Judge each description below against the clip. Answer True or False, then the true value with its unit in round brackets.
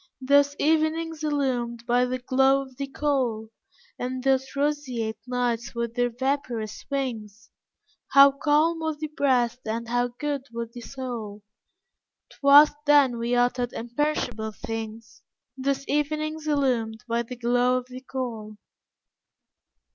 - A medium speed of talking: False (130 wpm)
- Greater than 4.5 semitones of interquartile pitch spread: False (3.2 semitones)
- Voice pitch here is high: True (255 Hz)